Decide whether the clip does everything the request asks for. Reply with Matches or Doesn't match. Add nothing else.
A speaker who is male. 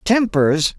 Matches